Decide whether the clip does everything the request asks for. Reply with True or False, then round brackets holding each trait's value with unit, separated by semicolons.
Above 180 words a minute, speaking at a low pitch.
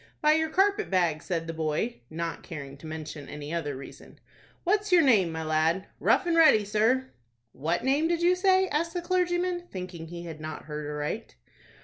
False (190 wpm; 185 Hz)